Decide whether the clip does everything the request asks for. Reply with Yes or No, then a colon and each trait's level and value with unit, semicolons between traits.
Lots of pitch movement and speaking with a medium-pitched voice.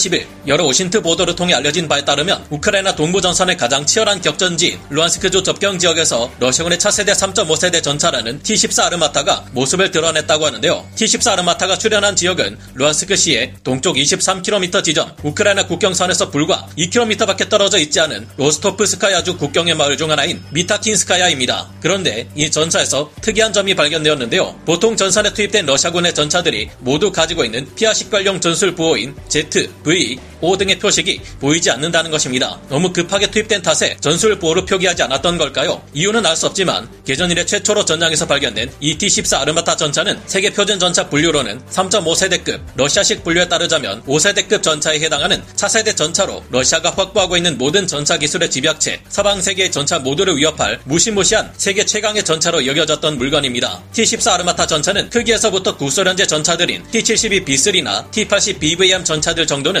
No: average, 4.8 semitones; medium, 175 Hz